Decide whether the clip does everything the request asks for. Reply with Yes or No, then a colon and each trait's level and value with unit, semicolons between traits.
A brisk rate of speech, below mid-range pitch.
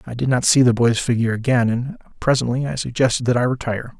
Yes: fast, 225 wpm; low, 120 Hz